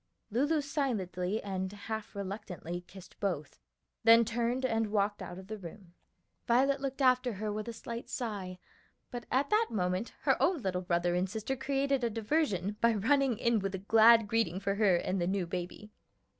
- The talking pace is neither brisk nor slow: Yes, average, 180 wpm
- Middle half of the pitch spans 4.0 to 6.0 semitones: Yes, average, 4.4 semitones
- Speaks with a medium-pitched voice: No, high, 215 Hz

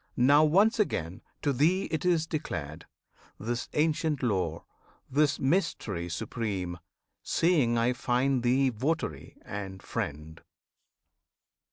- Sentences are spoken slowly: Yes, slow, 110 wpm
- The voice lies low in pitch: Yes, low, 125 Hz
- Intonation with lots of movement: Yes, wide, 8.3 semitones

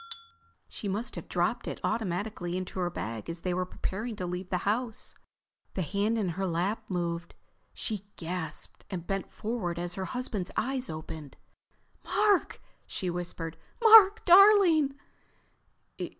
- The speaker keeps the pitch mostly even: No, average, 4.8 semitones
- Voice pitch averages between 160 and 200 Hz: Yes, high, 190 Hz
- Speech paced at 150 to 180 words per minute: No, average, 140 wpm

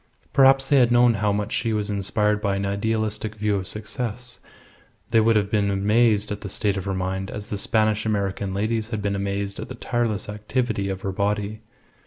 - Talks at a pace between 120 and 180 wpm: No, fast, 205 wpm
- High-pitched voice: No, low, 105 Hz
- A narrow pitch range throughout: Yes, narrow, 1.8 semitones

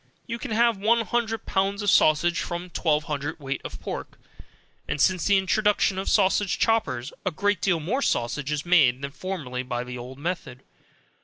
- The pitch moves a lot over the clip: Yes, wide, 6.3 semitones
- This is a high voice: No, medium, 175 Hz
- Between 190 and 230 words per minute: No, average, 180 wpm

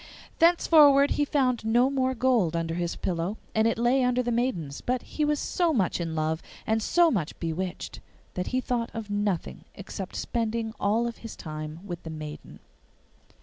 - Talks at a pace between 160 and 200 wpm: Yes, average, 175 wpm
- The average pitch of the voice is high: Yes, high, 225 Hz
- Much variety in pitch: Yes, wide, 6.8 semitones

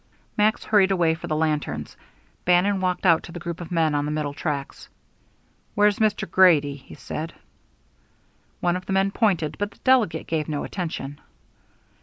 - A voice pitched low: No, medium, 175 Hz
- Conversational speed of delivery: Yes, average, 170 wpm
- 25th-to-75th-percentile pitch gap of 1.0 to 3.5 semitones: No, average, 4.1 semitones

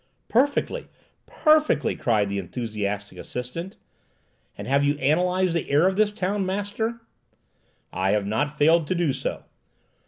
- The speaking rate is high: No, slow, 135 wpm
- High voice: No, medium, 155 Hz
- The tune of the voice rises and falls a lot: Yes, wide, 7.9 semitones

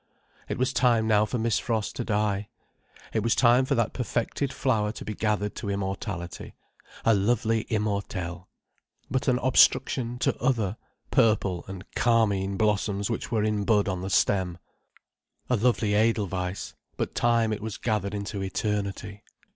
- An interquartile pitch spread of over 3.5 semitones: No, narrow, 2.6 semitones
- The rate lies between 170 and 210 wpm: No, average, 150 wpm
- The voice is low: Yes, low, 105 Hz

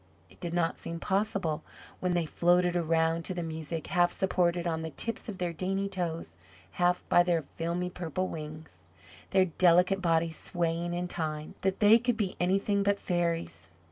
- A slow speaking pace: No, average, 175 wpm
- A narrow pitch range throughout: Yes, narrow, 2.2 semitones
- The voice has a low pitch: No, medium, 175 Hz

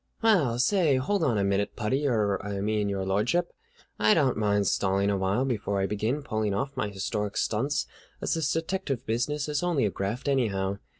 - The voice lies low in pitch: Yes, low, 110 Hz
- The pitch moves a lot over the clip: Yes, wide, 5.7 semitones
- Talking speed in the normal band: Yes, average, 185 wpm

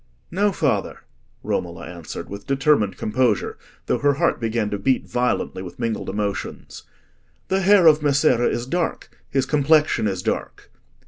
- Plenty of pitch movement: Yes, wide, 6.3 semitones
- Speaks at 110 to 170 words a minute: Yes, average, 140 wpm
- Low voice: Yes, low, 130 Hz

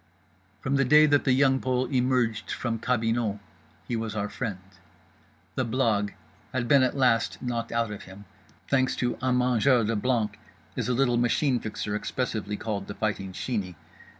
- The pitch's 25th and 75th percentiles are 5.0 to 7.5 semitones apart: No, average, 3.2 semitones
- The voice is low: Yes, low, 120 Hz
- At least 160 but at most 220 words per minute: Yes, average, 170 wpm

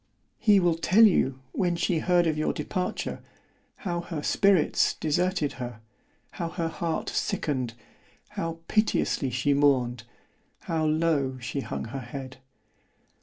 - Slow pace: Yes, slow, 115 wpm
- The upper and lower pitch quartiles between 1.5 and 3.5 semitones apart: No, average, 4.8 semitones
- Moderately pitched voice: Yes, medium, 155 Hz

